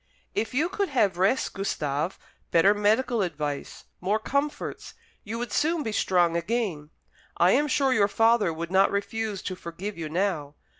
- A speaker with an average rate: Yes, average, 160 wpm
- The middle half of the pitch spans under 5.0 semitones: No, wide, 5.5 semitones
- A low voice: No, high, 200 Hz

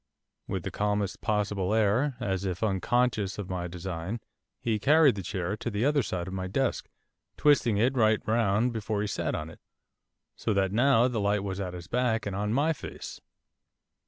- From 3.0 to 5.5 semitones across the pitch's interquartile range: Yes, average, 3.8 semitones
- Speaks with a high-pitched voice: No, low, 105 Hz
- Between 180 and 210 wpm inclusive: Yes, average, 190 wpm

